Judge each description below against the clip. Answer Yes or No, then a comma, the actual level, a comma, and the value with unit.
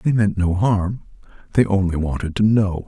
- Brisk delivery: No, average, 190 wpm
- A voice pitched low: Yes, low, 100 Hz